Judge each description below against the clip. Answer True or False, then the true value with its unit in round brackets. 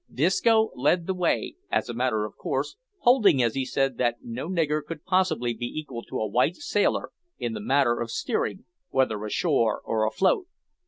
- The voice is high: False (135 Hz)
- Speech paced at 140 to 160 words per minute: False (180 wpm)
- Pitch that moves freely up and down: True (7.3 semitones)